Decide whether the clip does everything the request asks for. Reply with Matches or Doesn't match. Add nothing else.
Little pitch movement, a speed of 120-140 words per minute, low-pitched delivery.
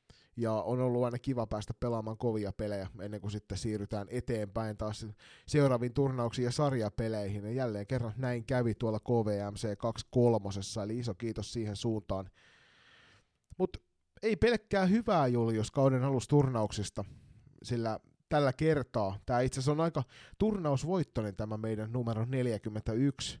Doesn't match